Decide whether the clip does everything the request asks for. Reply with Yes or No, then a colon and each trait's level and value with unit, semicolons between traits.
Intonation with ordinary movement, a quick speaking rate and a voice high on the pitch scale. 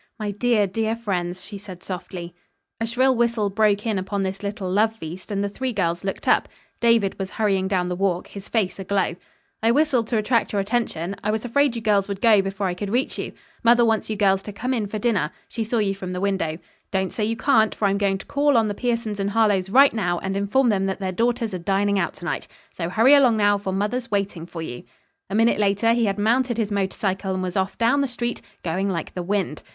Yes: average, 3.0 semitones; fast, 240 wpm; high, 205 Hz